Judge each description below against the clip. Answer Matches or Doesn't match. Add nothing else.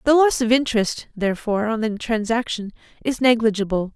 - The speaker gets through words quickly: Doesn't match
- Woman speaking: Matches